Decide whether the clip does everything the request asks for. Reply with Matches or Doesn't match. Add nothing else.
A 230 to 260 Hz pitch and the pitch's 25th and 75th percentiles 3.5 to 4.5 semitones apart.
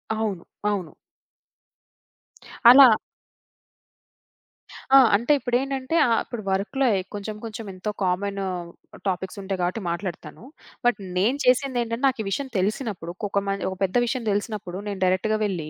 Doesn't match